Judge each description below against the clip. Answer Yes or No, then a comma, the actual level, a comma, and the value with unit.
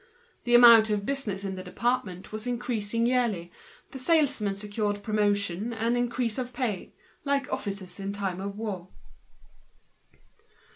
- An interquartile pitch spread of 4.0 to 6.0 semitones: No, average, 3.4 semitones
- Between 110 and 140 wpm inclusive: Yes, slow, 135 wpm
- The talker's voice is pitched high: Yes, high, 215 Hz